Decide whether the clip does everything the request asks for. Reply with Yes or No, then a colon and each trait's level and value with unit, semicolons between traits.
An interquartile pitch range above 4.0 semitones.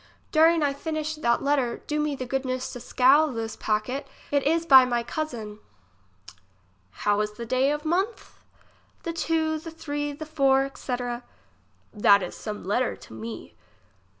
Yes: average, 4.7 semitones